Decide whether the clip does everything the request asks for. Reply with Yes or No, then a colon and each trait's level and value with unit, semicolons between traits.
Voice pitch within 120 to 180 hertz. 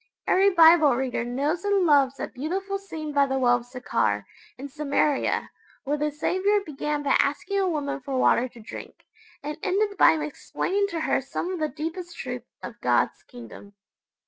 No: very high, 300 Hz